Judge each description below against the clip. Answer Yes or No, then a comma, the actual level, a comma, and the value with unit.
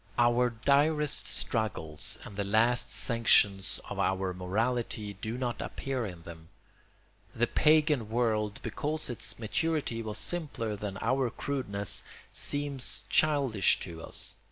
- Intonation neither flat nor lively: Yes, average, 4.9 semitones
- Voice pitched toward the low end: Yes, low, 115 Hz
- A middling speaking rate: No, slow, 125 wpm